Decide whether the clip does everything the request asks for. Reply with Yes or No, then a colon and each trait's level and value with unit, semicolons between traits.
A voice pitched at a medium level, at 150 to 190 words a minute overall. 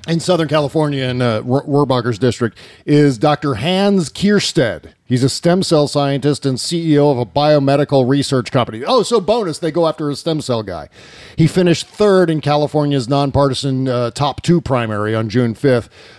Yes: medium, 145 Hz; average, 170 wpm